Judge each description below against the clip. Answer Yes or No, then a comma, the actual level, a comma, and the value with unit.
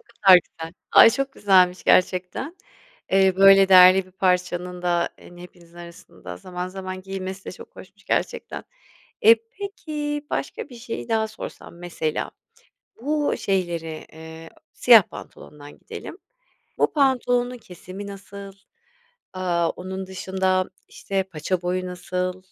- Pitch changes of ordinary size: No, narrow, 2.0 semitones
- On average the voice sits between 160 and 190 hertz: Yes, medium, 185 Hz